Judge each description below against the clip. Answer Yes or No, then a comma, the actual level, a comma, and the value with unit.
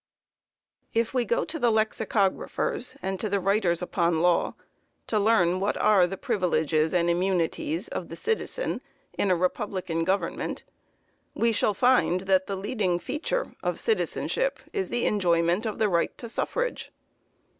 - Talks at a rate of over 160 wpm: No, average, 155 wpm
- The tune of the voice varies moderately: Yes, average, 4.7 semitones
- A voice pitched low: No, high, 195 Hz